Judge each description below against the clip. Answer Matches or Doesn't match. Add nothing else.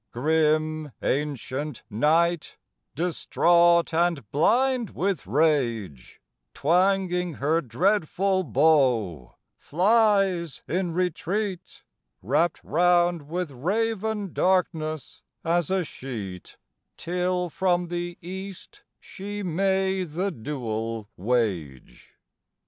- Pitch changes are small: Doesn't match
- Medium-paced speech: Doesn't match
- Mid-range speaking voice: Matches